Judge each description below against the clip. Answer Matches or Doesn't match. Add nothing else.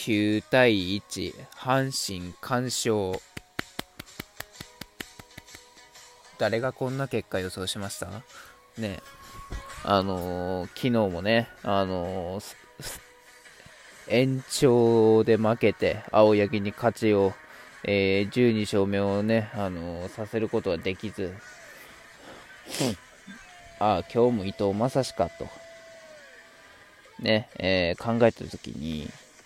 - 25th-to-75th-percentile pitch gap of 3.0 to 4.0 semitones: Matches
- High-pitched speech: Doesn't match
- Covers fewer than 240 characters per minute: Matches